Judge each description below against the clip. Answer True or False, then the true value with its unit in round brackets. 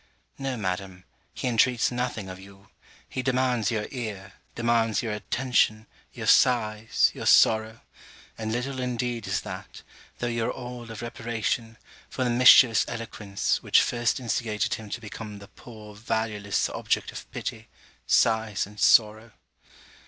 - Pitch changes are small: True (2.3 semitones)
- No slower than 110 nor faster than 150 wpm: True (140 wpm)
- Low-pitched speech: True (115 Hz)